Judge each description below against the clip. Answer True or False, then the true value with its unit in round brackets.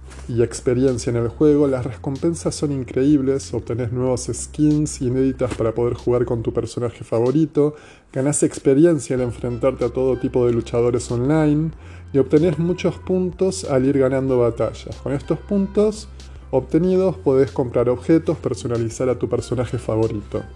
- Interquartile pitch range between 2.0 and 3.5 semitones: False (3.9 semitones)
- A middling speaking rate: True (145 wpm)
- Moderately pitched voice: False (130 Hz)